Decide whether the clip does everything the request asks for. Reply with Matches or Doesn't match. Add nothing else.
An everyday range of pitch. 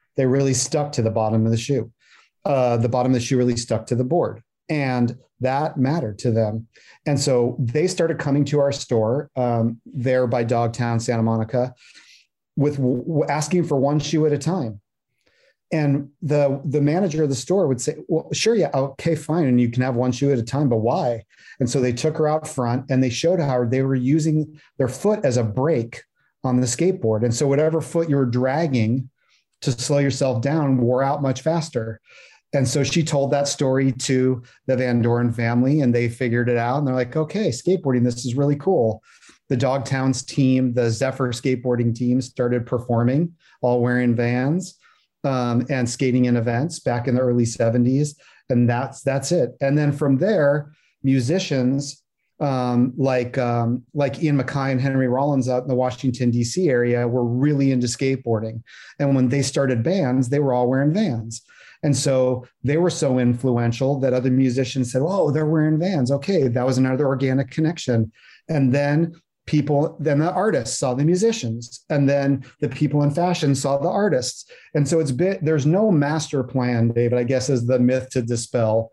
Matches